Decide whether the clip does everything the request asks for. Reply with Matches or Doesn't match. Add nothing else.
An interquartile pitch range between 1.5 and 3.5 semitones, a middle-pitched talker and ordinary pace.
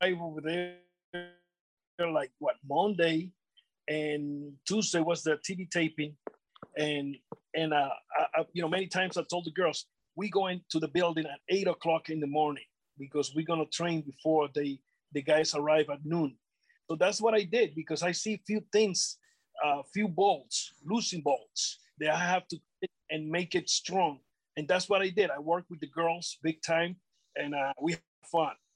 Matches